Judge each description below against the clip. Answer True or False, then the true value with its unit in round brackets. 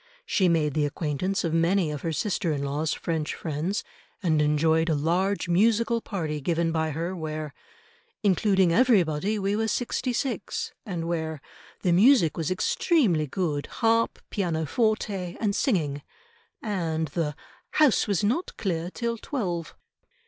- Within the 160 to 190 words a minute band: False (140 wpm)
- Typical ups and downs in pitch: True (4.6 semitones)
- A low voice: False (175 Hz)